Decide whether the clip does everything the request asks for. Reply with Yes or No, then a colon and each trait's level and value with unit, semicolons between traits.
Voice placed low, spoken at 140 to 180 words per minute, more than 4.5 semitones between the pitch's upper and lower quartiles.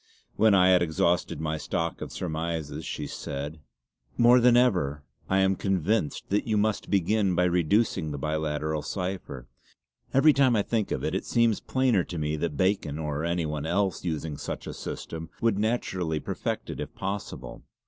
Yes: very low, 90 Hz; average, 175 wpm; average, 5.0 semitones